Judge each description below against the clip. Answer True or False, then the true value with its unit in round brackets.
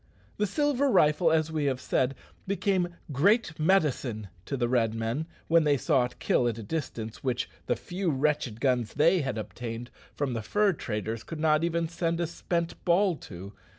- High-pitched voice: False (150 Hz)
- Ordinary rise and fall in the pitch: False (5.9 semitones)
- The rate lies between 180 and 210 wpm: True (185 wpm)